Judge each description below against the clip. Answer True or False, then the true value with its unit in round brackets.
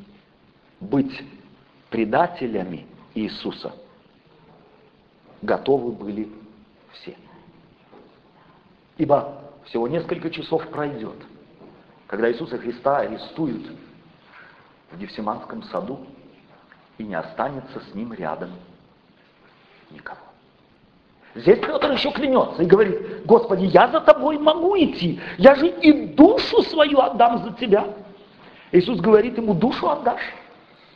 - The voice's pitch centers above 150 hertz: True (190 Hz)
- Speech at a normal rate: False (95 wpm)